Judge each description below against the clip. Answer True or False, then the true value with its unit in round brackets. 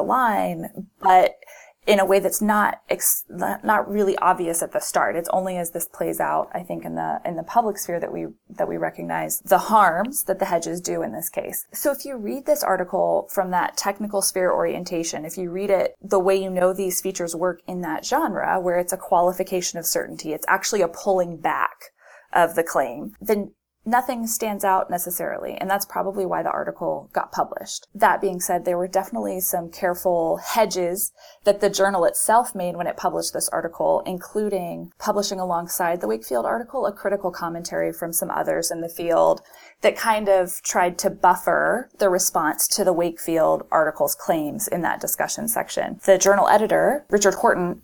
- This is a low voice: False (185 Hz)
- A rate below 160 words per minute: False (190 wpm)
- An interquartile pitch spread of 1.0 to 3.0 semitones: True (2.5 semitones)